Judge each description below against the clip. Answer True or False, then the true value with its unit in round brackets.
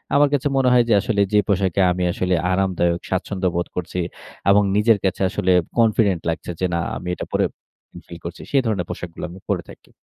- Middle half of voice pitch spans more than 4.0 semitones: False (3.0 semitones)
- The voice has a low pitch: True (95 Hz)